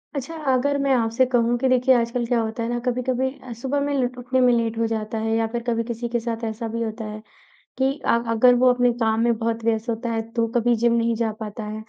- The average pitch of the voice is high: Yes, high, 235 Hz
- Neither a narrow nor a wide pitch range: No, narrow, 1.7 semitones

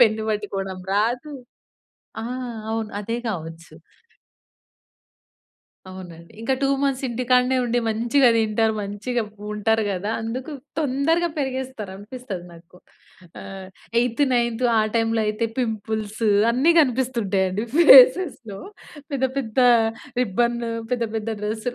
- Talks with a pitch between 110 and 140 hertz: No, high, 225 Hz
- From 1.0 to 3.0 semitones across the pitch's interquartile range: No, average, 3.4 semitones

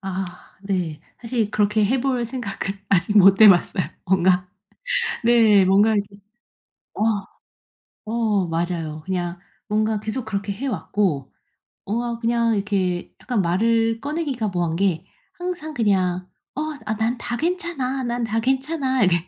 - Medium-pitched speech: No, high, 210 Hz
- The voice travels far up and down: No, average, 4.2 semitones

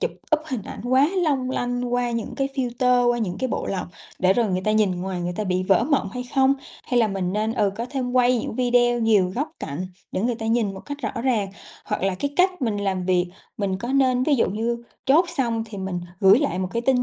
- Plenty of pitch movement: No, average, 4.6 semitones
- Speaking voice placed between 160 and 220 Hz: No, high, 235 Hz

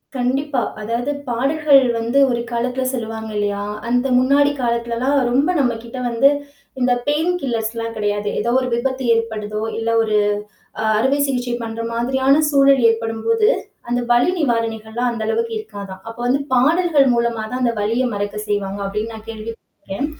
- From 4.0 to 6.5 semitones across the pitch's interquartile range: No, average, 3.2 semitones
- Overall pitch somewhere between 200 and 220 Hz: No, high, 235 Hz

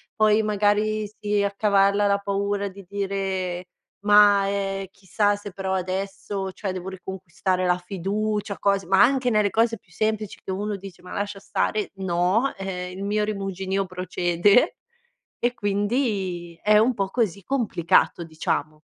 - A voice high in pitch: Yes, high, 200 Hz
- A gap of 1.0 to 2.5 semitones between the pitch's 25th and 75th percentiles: Yes, narrow, 1.8 semitones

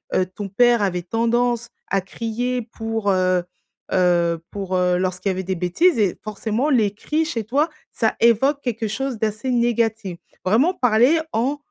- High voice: Yes, high, 220 Hz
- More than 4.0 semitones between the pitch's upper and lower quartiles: Yes, average, 4.4 semitones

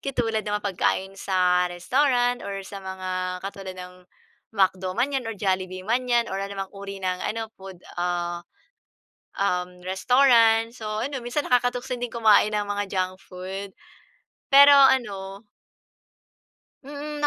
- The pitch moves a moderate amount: Yes, average, 4.6 semitones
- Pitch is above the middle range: Yes, high, 200 Hz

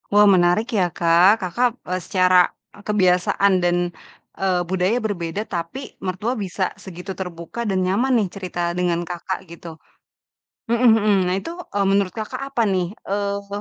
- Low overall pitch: No, high, 190 Hz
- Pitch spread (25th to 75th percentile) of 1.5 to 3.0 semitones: Yes, narrow, 2.6 semitones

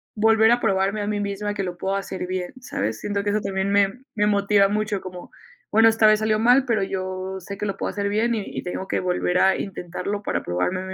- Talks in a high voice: Yes, high, 200 Hz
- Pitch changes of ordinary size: No, narrow, 2.1 semitones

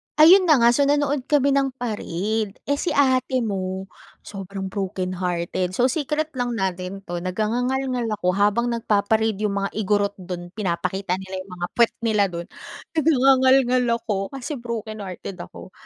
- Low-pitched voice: No, high, 215 Hz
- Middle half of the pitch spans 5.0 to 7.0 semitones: Yes, average, 5.3 semitones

